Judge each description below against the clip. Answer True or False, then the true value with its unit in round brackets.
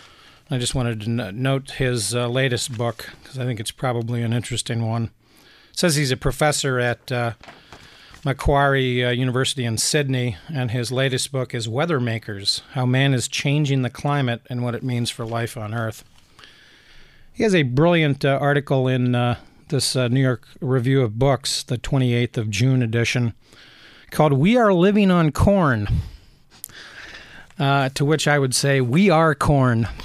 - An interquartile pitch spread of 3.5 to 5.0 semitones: False (2.9 semitones)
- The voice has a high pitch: False (130 Hz)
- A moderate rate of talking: True (170 wpm)